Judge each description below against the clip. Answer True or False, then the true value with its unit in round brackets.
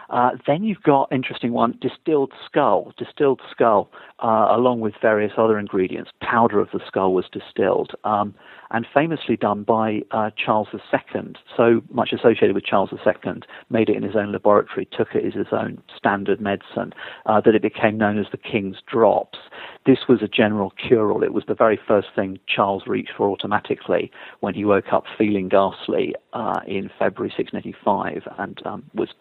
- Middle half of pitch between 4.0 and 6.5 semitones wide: False (3.0 semitones)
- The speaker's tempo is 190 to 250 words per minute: False (180 wpm)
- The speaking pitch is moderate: False (110 Hz)